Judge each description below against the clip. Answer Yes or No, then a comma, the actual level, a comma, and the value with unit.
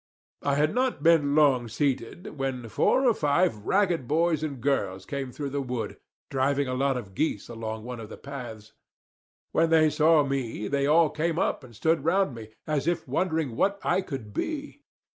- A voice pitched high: No, medium, 140 Hz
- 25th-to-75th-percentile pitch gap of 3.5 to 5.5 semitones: Yes, average, 4.7 semitones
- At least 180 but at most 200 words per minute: Yes, average, 185 wpm